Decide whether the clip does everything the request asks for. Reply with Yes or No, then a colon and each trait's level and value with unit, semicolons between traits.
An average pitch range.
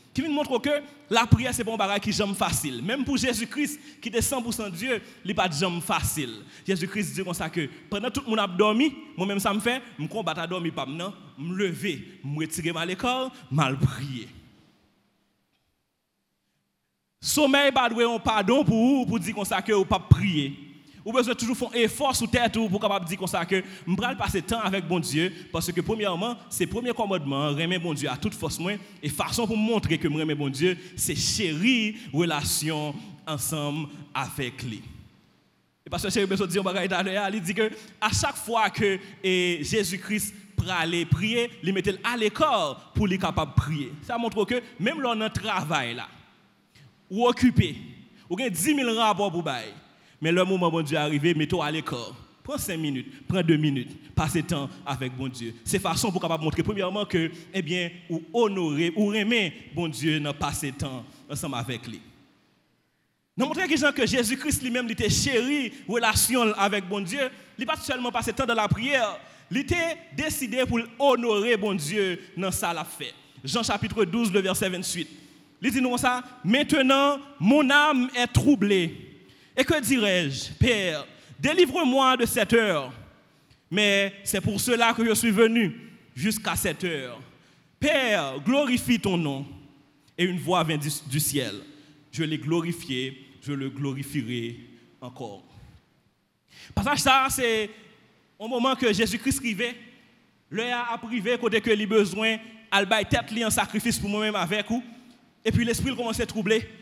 No: wide, 6.3 semitones